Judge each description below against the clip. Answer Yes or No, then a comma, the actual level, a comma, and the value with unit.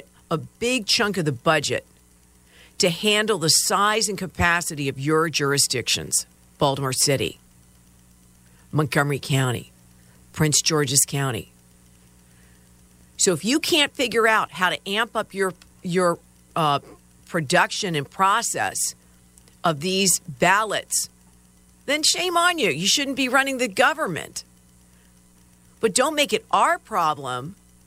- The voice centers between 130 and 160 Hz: Yes, medium, 140 Hz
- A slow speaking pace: Yes, slow, 125 wpm